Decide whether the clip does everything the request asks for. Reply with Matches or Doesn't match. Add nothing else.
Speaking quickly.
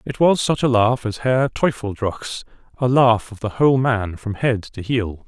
Doesn't match